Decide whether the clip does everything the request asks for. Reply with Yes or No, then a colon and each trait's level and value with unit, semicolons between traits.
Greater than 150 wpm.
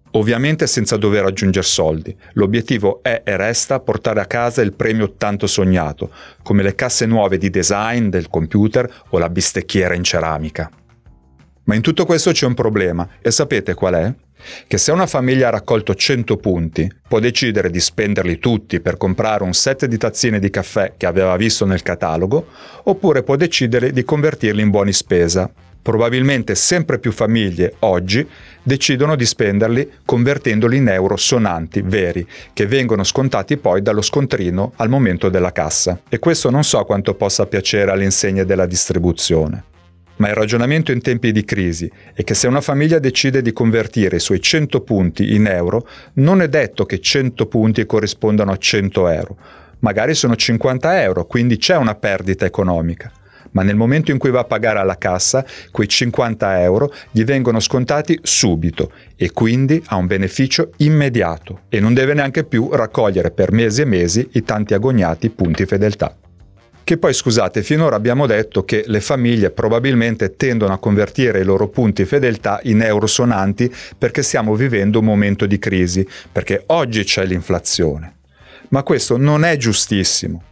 Yes: average, 165 wpm